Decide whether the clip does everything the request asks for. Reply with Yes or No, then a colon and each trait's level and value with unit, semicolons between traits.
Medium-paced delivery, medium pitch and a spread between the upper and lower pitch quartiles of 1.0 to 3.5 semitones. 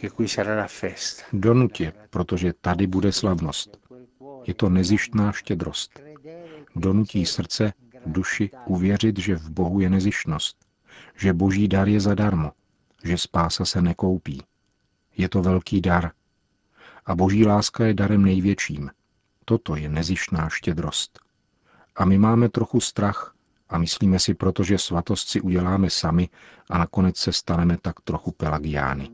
No: average, 125 wpm; very low, 95 Hz; average, 2.9 semitones